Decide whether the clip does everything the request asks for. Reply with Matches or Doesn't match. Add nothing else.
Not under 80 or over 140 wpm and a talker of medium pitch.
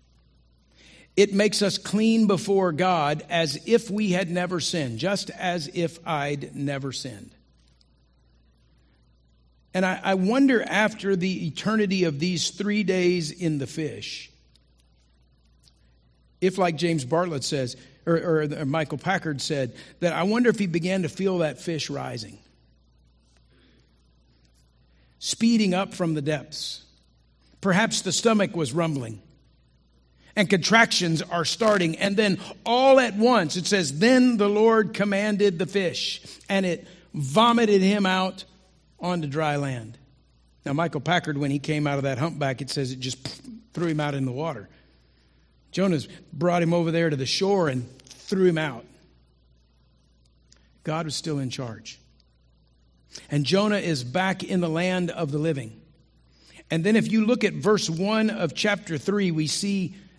Doesn't match